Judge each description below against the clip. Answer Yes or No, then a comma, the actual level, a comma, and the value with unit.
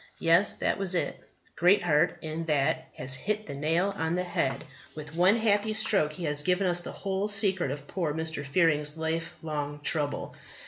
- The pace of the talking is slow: No, average, 180 wpm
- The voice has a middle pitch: Yes, medium, 165 Hz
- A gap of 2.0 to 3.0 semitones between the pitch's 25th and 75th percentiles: No, average, 4.3 semitones